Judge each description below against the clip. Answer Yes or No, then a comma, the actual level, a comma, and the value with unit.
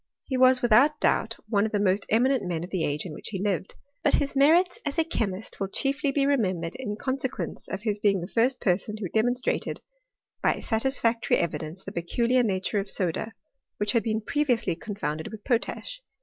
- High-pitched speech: Yes, high, 220 Hz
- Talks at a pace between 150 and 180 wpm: No, average, 200 wpm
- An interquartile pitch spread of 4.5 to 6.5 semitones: Yes, average, 5.2 semitones